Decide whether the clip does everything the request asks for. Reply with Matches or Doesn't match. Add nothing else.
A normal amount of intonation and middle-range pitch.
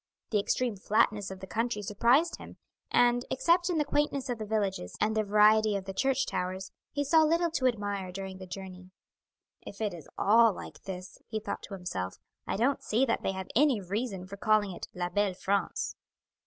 Doesn't match